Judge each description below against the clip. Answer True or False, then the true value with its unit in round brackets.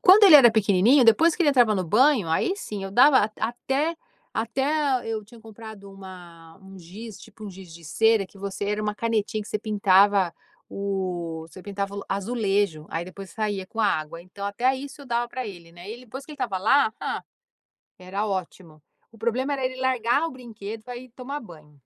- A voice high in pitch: True (215 Hz)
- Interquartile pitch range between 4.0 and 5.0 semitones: True (4.4 semitones)